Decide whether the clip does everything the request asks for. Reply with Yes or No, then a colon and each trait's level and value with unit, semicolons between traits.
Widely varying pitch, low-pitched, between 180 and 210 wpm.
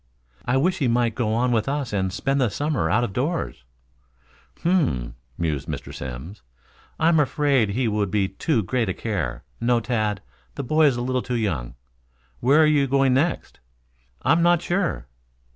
Yes: wide, 6.1 semitones; low, 120 Hz; average, 195 wpm